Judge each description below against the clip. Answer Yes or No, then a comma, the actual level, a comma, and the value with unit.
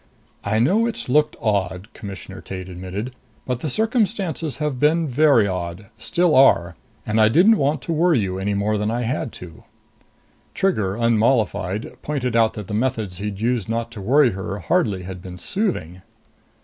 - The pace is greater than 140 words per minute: Yes, average, 170 wpm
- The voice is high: No, low, 115 Hz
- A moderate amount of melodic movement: No, wide, 7.4 semitones